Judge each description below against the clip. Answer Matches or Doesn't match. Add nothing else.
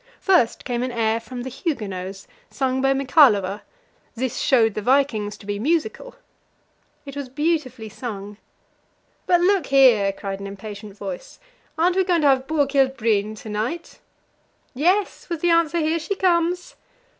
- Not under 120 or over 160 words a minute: Matches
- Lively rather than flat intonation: Matches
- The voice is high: Matches